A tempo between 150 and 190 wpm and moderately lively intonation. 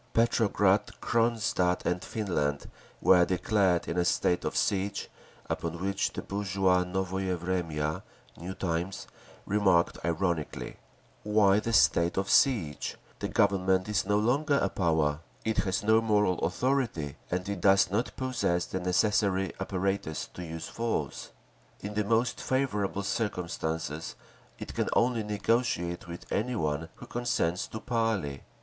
No: slow, 135 wpm; average, 3.5 semitones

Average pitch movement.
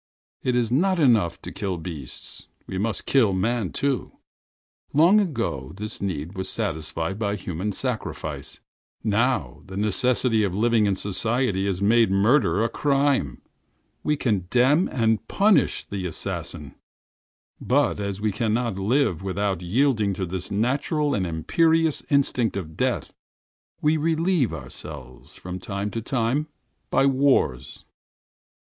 No: wide, 5.9 semitones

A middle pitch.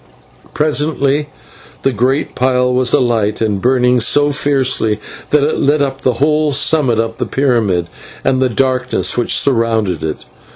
No: low, 130 Hz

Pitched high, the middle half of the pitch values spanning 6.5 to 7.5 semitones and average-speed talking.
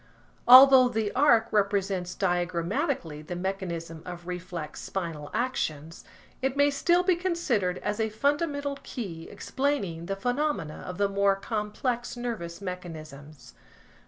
No: high, 200 Hz; wide, 6.9 semitones; slow, 125 wpm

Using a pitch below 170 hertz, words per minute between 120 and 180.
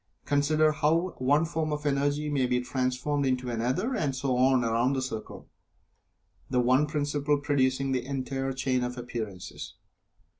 Yes: low, 135 Hz; average, 150 wpm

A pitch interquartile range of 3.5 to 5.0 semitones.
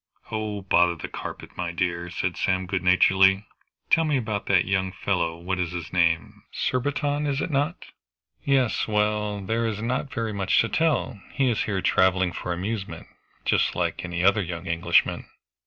Yes: average, 4.1 semitones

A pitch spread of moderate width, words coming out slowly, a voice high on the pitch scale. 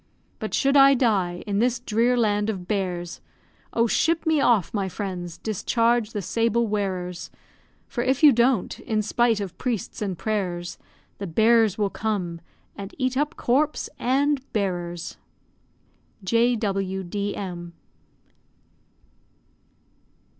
Yes: average, 4.2 semitones; slow, 120 wpm; high, 215 Hz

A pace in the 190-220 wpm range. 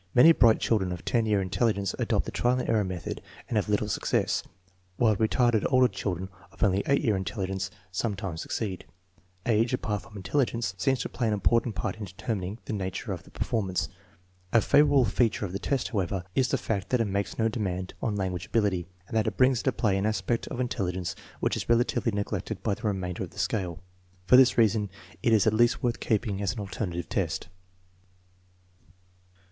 Yes: average, 200 wpm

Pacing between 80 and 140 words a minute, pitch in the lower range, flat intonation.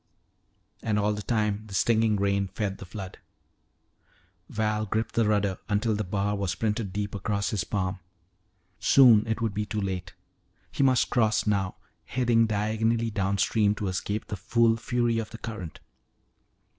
No: average, 155 wpm; low, 105 Hz; narrow, 2.1 semitones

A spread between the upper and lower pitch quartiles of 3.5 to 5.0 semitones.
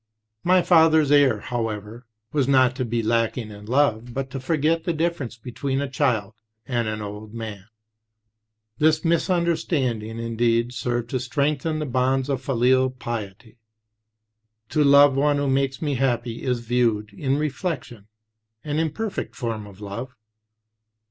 Yes: average, 3.9 semitones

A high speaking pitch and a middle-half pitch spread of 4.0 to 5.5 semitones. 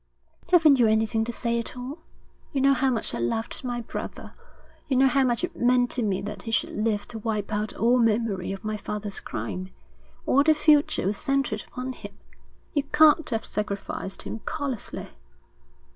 Yes: high, 235 Hz; average, 4.3 semitones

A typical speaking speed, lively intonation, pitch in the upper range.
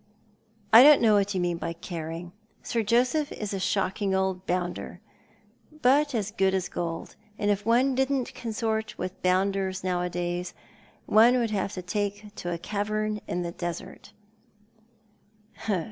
No: average, 155 wpm; average, 3.4 semitones; high, 200 Hz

